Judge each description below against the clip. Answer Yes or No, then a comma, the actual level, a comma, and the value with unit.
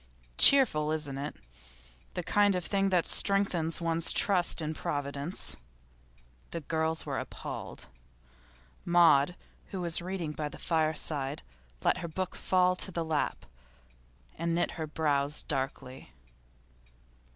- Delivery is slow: Yes, slow, 125 wpm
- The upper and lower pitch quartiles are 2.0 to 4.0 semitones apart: Yes, average, 3.1 semitones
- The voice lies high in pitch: No, medium, 165 Hz